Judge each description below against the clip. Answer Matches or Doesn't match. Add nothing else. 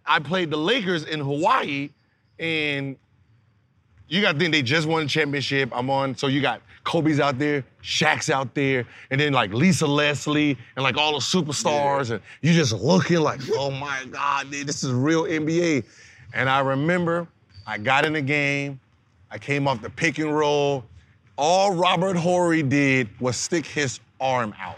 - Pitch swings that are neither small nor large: Matches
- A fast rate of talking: Doesn't match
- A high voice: Doesn't match